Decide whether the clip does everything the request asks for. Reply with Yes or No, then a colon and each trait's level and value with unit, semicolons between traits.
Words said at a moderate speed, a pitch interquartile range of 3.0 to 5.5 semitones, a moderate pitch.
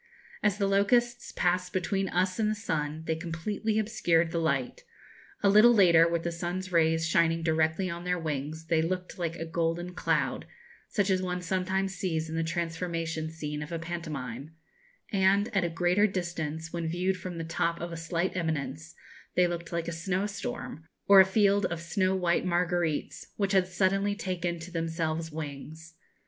No: average, 180 wpm; narrow, 2.6 semitones; medium, 170 Hz